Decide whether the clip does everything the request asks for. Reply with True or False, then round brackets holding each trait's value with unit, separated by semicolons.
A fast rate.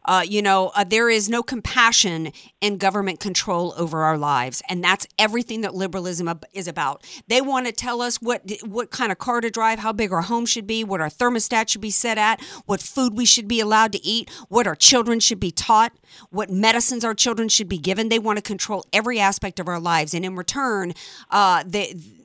True (220 wpm)